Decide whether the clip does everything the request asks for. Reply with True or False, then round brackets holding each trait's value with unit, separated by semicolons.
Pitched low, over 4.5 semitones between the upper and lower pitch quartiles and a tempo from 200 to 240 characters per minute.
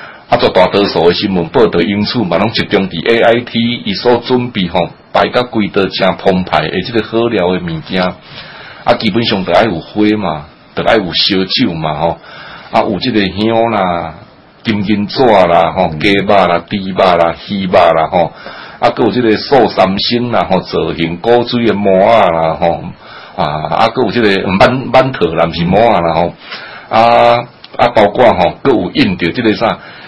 False (100 Hz; 4.9 semitones; 255 characters per minute)